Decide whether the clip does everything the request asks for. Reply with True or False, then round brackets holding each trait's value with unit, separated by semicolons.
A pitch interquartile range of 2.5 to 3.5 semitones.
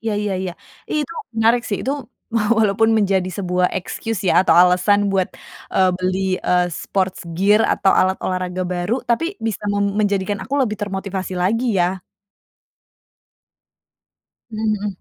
True (2.9 semitones)